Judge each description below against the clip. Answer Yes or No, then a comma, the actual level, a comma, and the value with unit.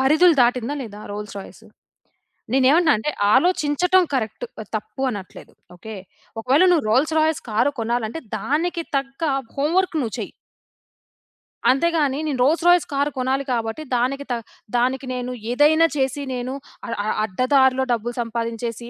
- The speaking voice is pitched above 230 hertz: Yes, very high, 265 Hz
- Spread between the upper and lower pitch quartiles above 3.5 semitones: Yes, average, 4.4 semitones